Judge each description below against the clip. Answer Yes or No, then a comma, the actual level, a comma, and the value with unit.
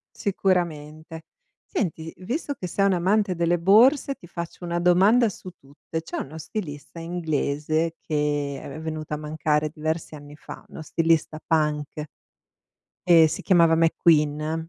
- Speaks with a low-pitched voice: No, medium, 165 Hz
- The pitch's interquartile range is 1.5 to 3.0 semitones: Yes, average, 2.7 semitones